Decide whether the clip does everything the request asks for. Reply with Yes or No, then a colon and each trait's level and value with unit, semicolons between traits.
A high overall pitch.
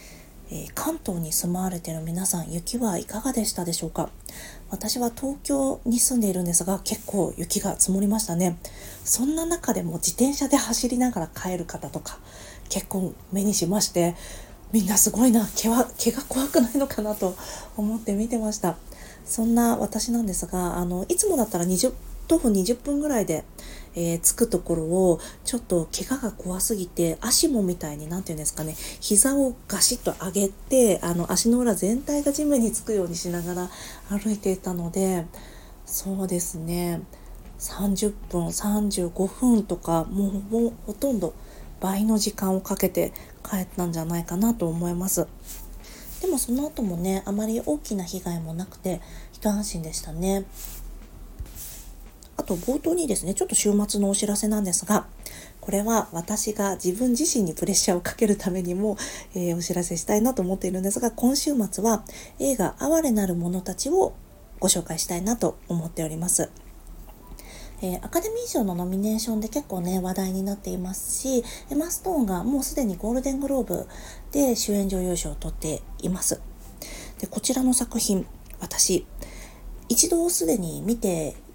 Yes: high, 195 Hz